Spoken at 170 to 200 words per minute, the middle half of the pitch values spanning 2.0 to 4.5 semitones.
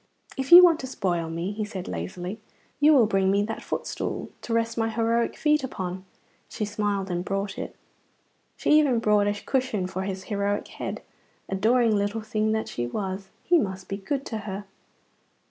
Yes: average, 180 wpm; average, 3.3 semitones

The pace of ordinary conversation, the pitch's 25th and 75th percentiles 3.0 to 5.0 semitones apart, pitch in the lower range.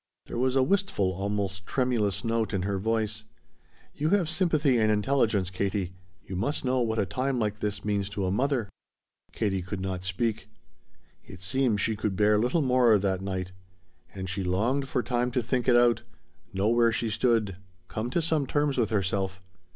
Yes: average, 180 wpm; average, 4.5 semitones; low, 110 Hz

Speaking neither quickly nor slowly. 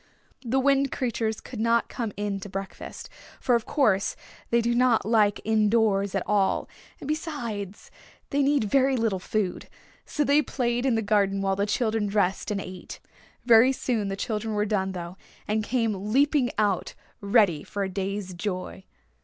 Yes: average, 170 wpm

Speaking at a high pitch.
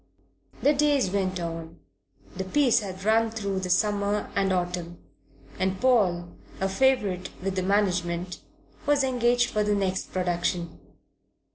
Yes: high, 195 Hz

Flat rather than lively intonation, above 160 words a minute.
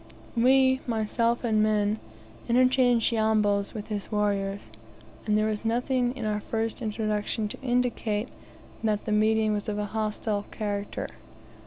No: narrow, 2.1 semitones; average, 140 wpm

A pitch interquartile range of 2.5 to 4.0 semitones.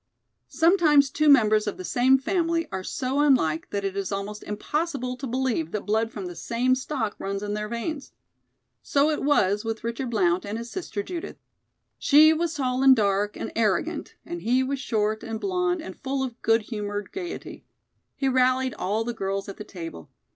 No: average, 5.1 semitones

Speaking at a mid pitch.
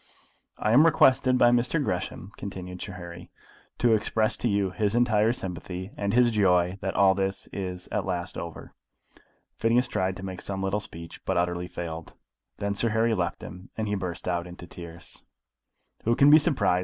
No: very low, 95 Hz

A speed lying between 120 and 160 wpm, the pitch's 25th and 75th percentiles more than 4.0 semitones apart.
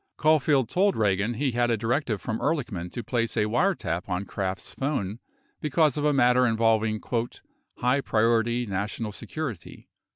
Yes: average, 150 wpm; average, 4.4 semitones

